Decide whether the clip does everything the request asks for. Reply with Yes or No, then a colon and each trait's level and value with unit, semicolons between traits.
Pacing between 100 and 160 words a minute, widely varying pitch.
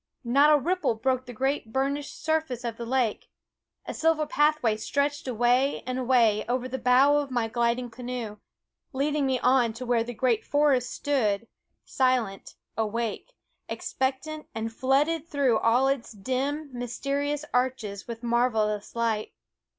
No: average, 145 wpm; average, 3.3 semitones